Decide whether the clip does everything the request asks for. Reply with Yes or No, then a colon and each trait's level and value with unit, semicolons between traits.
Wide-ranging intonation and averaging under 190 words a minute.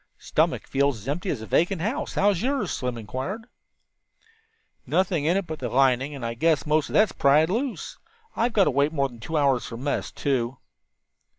No: wide, 6.3 semitones; average, 195 wpm